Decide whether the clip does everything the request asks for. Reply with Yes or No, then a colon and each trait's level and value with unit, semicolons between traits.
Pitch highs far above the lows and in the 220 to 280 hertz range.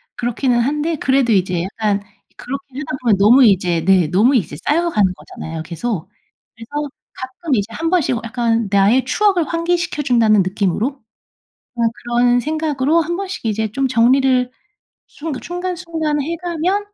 Yes: wide, 6.4 semitones; very high, 255 Hz